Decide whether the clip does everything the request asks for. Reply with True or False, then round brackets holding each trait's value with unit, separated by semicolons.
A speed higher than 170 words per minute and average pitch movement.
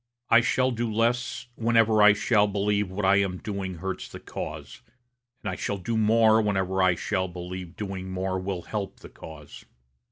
True (180 wpm; 3.0 semitones)